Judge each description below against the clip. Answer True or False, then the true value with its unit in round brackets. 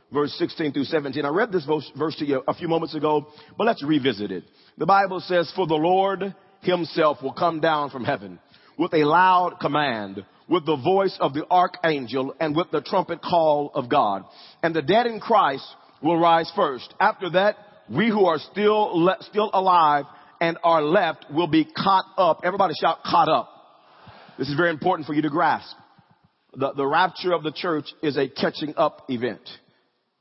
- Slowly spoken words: False (185 wpm)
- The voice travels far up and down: False (3.7 semitones)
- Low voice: False (165 Hz)